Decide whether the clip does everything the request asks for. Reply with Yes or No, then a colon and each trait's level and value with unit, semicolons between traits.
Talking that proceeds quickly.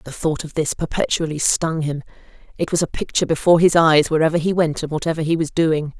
Yes: fast, 220 wpm